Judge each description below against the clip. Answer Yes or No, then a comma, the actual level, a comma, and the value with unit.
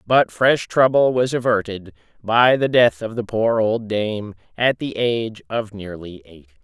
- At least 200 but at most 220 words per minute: No, average, 170 wpm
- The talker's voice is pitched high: No, low, 110 Hz